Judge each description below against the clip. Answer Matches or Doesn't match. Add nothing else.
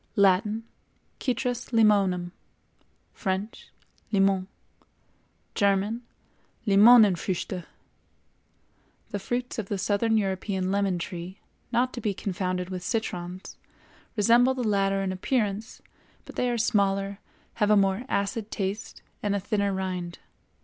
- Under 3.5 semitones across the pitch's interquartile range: Matches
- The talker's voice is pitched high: Matches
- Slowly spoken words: Matches